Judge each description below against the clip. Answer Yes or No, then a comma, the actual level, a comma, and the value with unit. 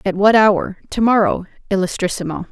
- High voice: Yes, high, 195 Hz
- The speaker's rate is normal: Yes, average, 145 wpm